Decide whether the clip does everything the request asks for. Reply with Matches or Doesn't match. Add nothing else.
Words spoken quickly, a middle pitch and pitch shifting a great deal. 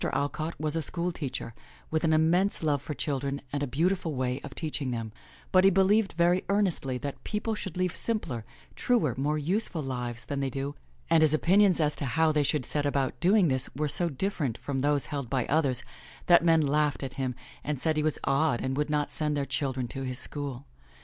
Doesn't match